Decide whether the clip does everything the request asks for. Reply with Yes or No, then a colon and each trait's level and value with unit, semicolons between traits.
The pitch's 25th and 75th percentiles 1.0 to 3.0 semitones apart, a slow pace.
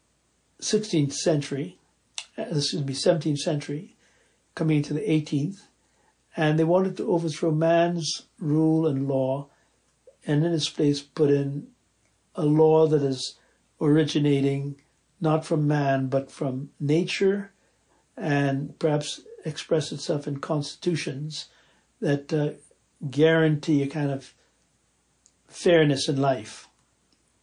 Yes: narrow, 2.4 semitones; slow, 115 wpm